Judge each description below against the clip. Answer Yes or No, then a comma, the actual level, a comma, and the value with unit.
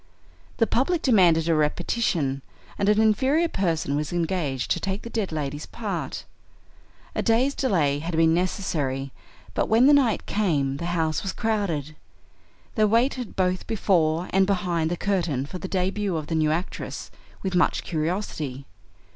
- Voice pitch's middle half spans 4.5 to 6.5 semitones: Yes, average, 5.3 semitones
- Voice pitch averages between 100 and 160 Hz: No, medium, 180 Hz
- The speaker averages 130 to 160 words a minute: Yes, average, 155 wpm